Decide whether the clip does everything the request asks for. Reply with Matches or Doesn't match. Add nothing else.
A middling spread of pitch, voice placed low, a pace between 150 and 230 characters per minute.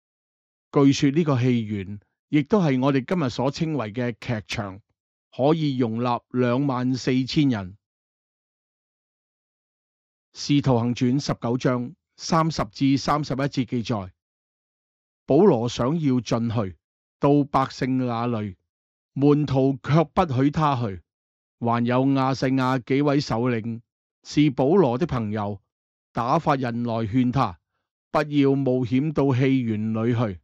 Matches